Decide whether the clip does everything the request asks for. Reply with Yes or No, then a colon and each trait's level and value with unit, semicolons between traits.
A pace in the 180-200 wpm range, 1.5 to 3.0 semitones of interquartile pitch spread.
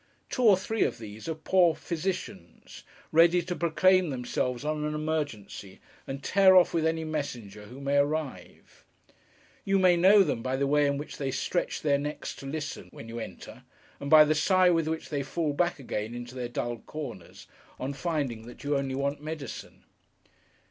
No: average, 185 wpm; average, 4.2 semitones